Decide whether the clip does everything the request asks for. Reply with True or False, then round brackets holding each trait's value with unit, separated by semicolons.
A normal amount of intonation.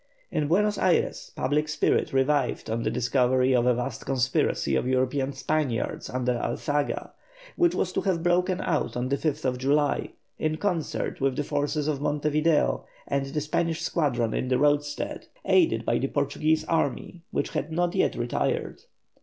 True (3.5 semitones)